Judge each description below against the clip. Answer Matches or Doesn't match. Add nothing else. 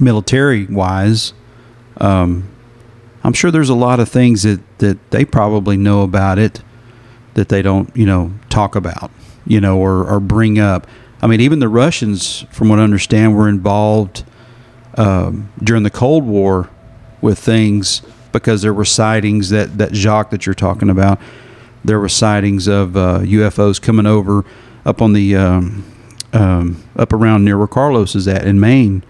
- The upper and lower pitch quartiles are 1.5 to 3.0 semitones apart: Matches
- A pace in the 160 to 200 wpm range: Matches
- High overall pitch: Doesn't match